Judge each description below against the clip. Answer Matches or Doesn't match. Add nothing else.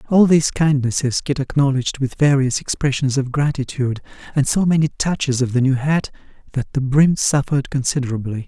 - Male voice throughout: Matches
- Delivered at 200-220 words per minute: Doesn't match